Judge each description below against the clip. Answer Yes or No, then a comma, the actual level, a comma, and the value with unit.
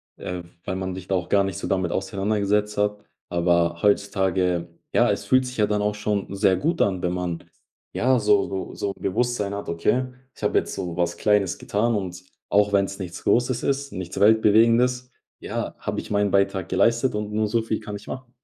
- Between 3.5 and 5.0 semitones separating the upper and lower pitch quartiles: No, narrow, 2.6 semitones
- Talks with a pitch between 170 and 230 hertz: No, low, 100 Hz